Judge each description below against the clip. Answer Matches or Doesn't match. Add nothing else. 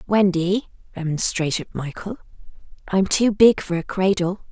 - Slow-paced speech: Matches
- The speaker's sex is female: Matches